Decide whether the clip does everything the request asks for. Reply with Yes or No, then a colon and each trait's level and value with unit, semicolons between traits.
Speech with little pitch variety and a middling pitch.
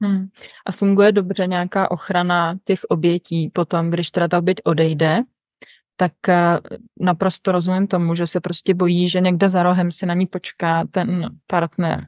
Yes: narrow, 1.6 semitones; medium, 180 Hz